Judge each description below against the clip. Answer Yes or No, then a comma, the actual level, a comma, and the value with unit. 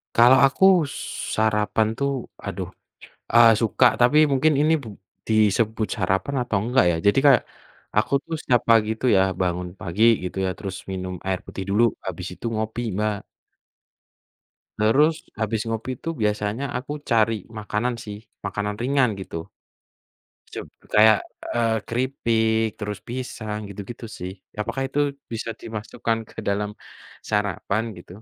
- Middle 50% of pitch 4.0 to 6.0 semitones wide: No, average, 2.7 semitones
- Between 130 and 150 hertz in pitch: No, low, 110 Hz